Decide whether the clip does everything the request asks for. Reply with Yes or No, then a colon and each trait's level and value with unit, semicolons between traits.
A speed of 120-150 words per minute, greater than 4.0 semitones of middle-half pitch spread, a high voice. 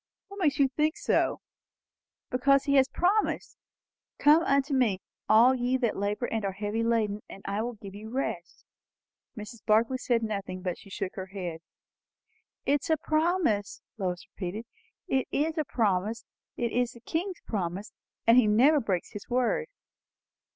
No: average, 165 wpm; average, 5.2 semitones; high, 235 Hz